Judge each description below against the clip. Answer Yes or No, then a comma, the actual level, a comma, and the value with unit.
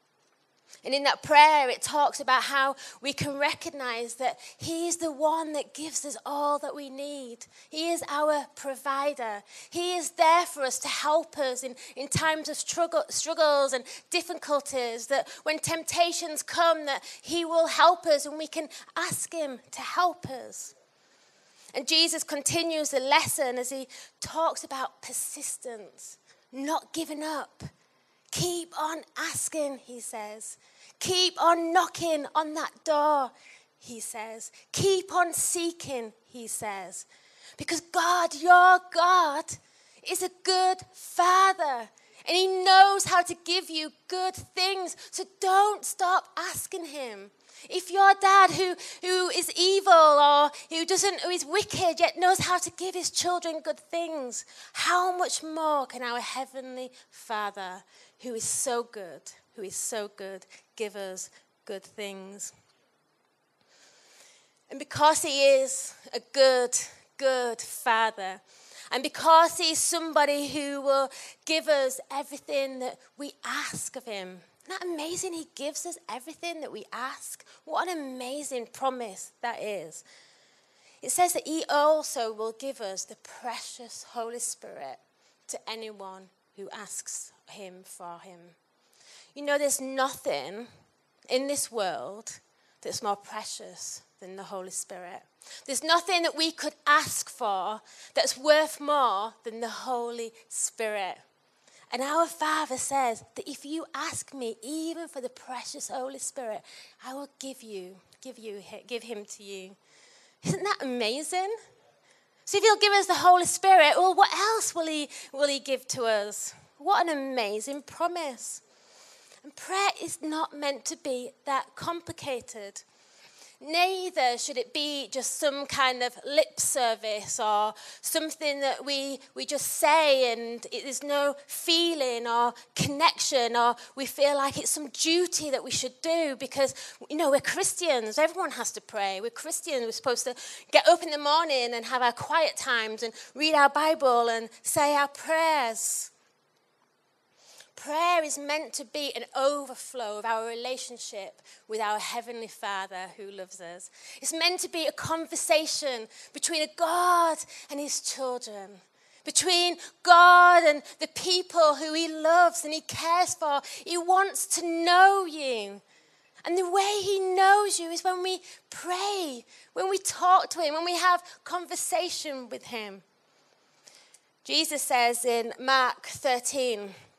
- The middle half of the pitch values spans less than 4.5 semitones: No, average, 5.3 semitones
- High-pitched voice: Yes, very high, 290 Hz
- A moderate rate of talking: Yes, average, 150 wpm